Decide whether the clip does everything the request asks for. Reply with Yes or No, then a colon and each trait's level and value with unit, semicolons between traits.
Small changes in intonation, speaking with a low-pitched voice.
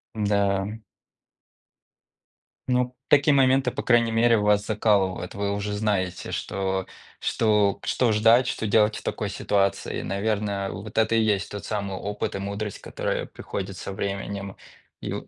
Yes: narrow, 2.2 semitones; low, 105 Hz